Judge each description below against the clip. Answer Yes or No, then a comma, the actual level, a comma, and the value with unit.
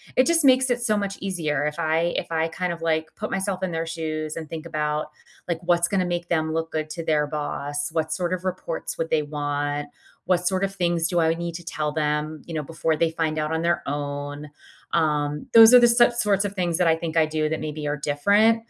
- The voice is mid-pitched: Yes, medium, 165 Hz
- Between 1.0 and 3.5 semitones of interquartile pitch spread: Yes, average, 2.9 semitones